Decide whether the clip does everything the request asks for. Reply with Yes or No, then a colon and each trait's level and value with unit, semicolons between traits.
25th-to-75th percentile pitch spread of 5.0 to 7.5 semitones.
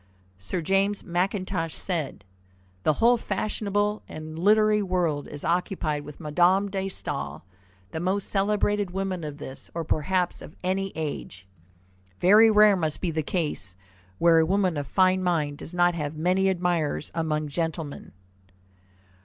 No: average, 3.8 semitones